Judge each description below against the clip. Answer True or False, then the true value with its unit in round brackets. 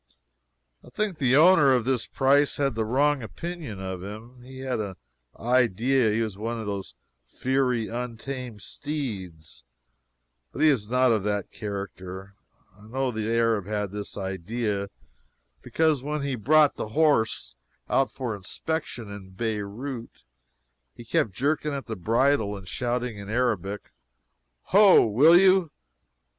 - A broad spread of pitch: False (4.8 semitones)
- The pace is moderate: True (145 wpm)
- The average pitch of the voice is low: True (120 Hz)